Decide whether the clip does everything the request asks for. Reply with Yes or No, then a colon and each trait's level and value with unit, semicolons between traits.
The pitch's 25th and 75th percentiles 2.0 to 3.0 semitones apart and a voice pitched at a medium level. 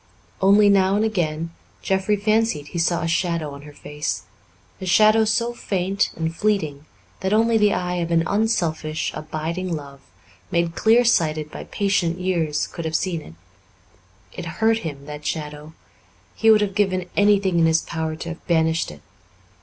No: average, 4.4 semitones; medium, 170 Hz